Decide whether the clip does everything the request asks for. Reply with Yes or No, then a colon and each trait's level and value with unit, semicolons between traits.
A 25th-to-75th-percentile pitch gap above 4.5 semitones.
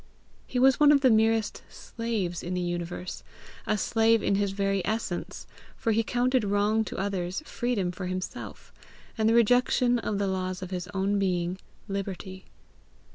No: average, 3.5 semitones